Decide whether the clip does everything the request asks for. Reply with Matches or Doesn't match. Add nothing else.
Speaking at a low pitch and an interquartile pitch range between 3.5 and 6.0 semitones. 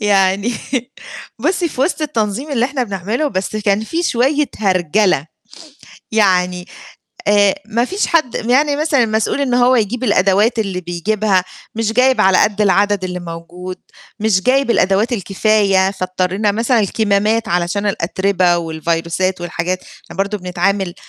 Doesn't match